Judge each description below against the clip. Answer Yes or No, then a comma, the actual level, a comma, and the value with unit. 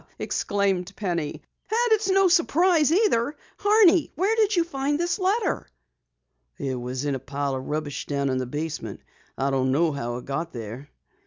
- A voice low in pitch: No, medium, 180 Hz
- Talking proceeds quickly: No, average, 170 wpm